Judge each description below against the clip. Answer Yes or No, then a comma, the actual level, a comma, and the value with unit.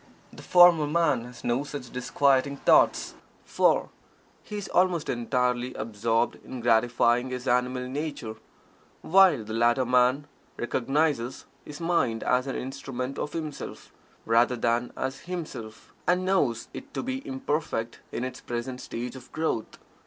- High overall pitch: No, low, 130 Hz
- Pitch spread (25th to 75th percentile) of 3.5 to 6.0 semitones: Yes, average, 4.1 semitones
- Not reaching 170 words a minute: Yes, average, 140 wpm